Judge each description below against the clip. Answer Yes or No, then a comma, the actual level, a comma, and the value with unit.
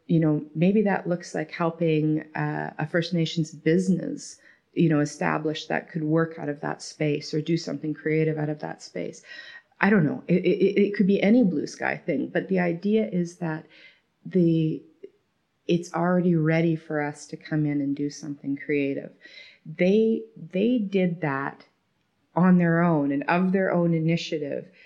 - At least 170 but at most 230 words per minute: Yes, average, 175 wpm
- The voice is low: No, medium, 165 Hz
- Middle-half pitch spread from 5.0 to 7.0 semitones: No, average, 2.7 semitones